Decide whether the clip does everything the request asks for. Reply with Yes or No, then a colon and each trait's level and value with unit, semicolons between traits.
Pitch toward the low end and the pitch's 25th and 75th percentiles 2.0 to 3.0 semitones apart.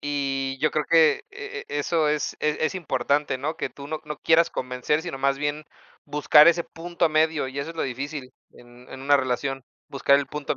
No: medium, 145 Hz; narrow, 2.4 semitones